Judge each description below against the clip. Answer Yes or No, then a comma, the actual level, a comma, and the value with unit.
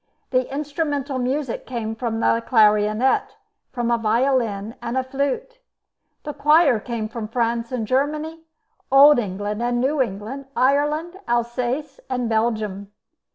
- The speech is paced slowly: Yes, slow, 130 wpm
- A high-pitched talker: Yes, high, 245 Hz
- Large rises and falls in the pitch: No, average, 3.8 semitones